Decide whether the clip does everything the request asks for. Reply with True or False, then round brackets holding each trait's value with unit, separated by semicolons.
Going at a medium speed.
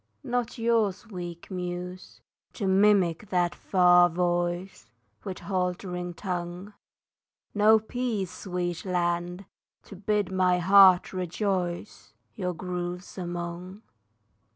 False (100 wpm)